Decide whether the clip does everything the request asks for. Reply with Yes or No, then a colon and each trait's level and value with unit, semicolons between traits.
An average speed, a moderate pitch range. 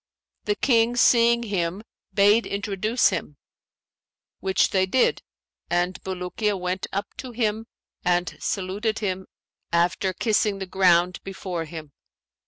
No: slow, 120 wpm; average, 3.1 semitones